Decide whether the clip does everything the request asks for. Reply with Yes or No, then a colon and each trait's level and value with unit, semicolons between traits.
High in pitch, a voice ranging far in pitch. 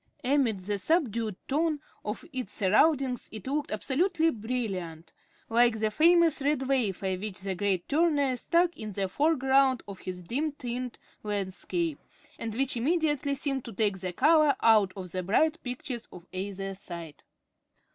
Yes: high, 240 Hz; wide, 6.6 semitones